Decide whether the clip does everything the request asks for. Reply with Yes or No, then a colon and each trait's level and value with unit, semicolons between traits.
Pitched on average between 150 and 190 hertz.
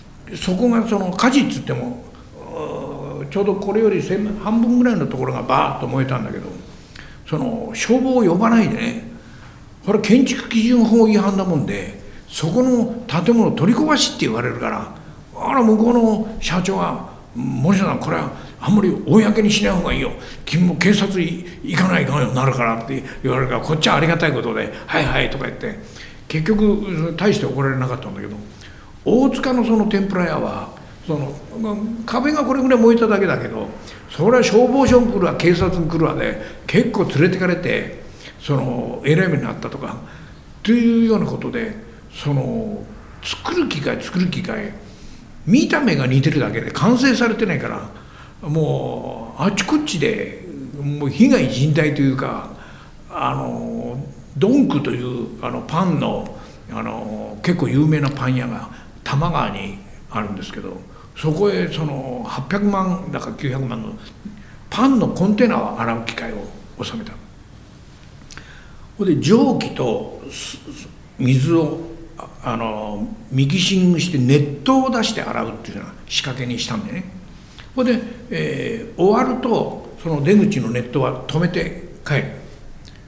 Yes: medium, 185 Hz